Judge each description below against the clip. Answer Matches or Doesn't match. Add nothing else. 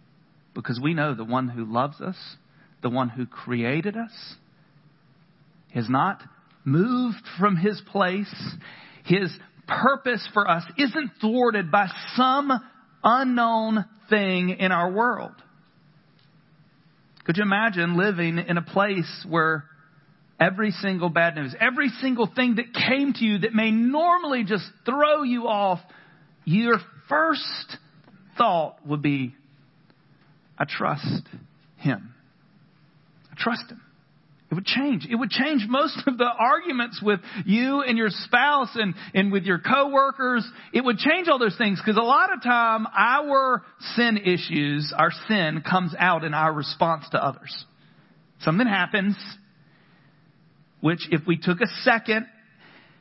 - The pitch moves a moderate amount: Doesn't match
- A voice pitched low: Doesn't match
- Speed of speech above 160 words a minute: Doesn't match